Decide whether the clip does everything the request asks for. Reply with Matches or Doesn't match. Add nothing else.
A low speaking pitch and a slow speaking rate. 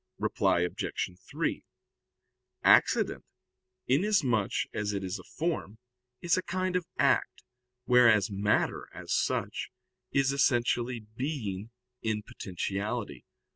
Matches